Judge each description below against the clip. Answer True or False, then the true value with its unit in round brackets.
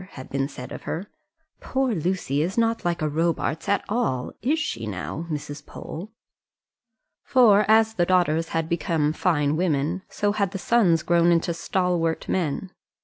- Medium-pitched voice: True (170 Hz)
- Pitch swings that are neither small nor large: True (4.5 semitones)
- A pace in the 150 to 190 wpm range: True (160 wpm)